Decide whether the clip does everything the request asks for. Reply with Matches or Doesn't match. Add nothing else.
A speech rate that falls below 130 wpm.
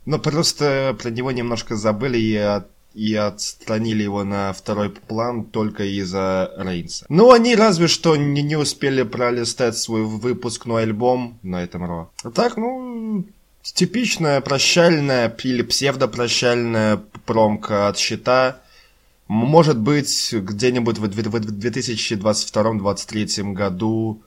Matches